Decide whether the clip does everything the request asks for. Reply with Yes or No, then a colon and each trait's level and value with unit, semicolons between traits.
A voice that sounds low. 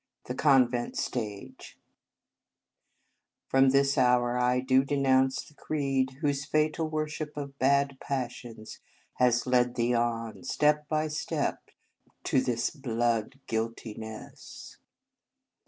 Yes: low, 130 Hz